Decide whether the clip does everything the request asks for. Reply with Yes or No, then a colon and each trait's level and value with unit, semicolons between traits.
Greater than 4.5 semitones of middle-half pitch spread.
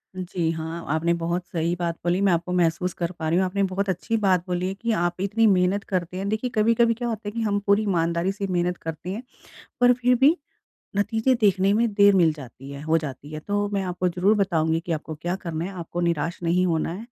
No: average, 3.2 semitones